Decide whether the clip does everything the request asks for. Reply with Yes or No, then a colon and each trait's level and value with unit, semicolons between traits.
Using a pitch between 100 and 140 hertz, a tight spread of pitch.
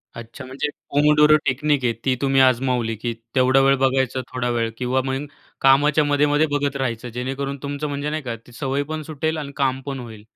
Yes: low, 135 Hz; narrow, 2.2 semitones